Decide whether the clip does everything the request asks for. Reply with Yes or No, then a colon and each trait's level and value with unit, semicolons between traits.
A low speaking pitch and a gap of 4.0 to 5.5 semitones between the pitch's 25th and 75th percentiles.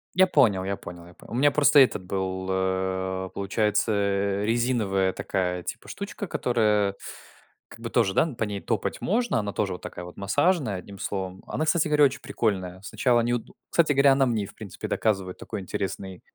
Yes: low, 100 Hz; average, 5.2 semitones